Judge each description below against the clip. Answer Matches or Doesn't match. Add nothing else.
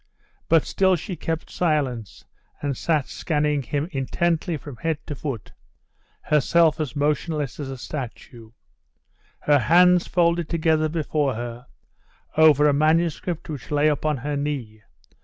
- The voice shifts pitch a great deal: Doesn't match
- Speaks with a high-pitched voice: Doesn't match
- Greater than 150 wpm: Doesn't match